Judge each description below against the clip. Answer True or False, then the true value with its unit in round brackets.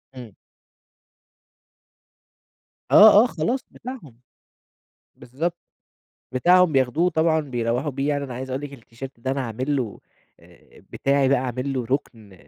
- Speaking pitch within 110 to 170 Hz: True (135 Hz)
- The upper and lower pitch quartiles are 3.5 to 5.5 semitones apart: True (3.9 semitones)